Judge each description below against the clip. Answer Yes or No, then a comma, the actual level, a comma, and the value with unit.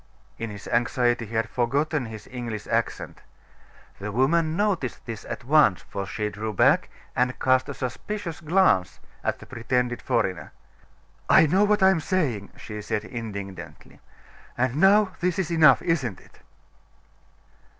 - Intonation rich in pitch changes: Yes, wide, 6.7 semitones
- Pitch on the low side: Yes, low, 125 Hz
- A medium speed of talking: Yes, average, 150 wpm